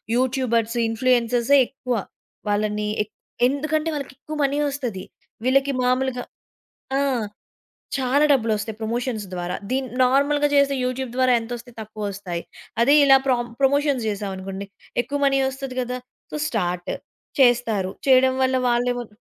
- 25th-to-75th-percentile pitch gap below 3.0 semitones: No, average, 3.5 semitones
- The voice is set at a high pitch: Yes, very high, 250 Hz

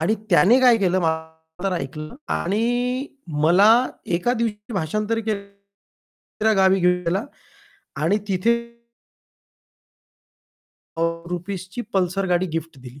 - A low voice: No, high, 190 Hz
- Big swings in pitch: No, average, 3.9 semitones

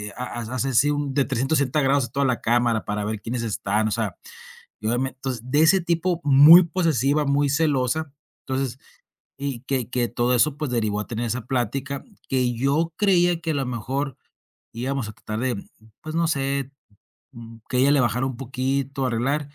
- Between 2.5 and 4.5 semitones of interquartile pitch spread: Yes, average, 3.1 semitones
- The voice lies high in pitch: No, low, 135 Hz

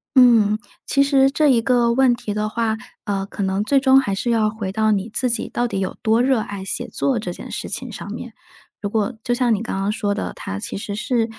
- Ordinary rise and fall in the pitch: Yes, average, 3.3 semitones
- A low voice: No, high, 220 Hz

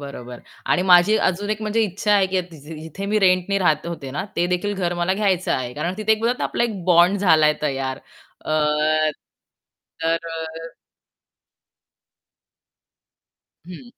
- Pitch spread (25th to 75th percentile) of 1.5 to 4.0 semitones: Yes, average, 3.7 semitones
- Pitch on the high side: No, medium, 180 Hz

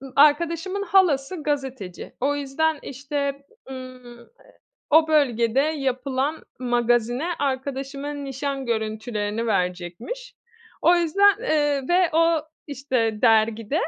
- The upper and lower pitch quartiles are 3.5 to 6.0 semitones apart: Yes, average, 4.4 semitones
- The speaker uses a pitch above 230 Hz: Yes, very high, 275 Hz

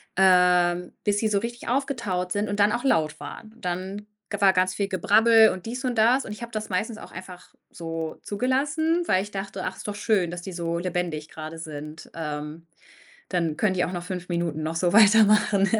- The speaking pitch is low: No, high, 190 Hz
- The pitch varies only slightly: No, average, 3.8 semitones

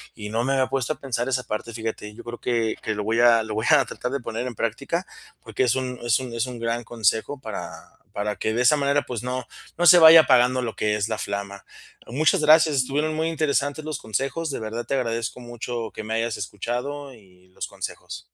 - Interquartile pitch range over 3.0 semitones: Yes, average, 3.7 semitones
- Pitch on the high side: No, low, 120 Hz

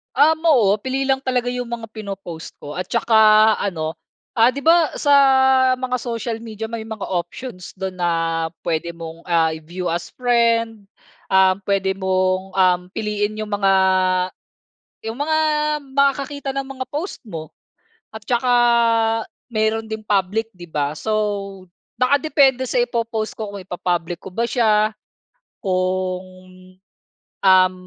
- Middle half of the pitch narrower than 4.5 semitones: No, average, 4.9 semitones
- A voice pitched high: Yes, high, 215 Hz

